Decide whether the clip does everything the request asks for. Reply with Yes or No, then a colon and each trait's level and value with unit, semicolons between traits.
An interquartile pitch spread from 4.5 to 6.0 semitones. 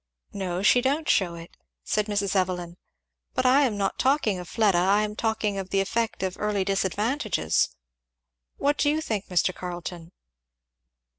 No: average, 3.5 semitones